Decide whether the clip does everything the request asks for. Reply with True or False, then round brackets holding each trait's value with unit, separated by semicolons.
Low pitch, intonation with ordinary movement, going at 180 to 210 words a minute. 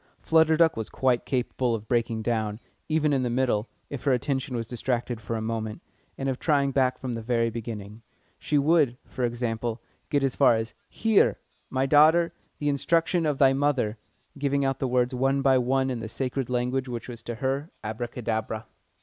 True (125 Hz; 3.1 semitones; 190 wpm)